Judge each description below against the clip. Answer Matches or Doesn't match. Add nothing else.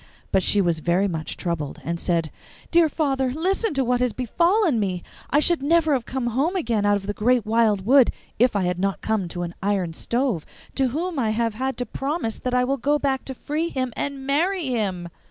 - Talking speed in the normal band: Doesn't match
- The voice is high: Matches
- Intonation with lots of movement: Matches